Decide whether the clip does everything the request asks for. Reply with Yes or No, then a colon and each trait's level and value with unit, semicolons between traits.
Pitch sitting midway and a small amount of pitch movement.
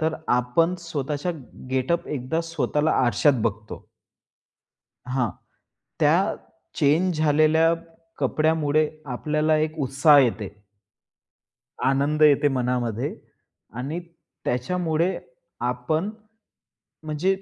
No: medium, 150 Hz; average, 3.9 semitones